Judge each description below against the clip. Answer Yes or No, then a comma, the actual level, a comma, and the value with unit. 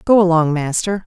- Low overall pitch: No, medium, 175 Hz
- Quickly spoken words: No, average, 160 wpm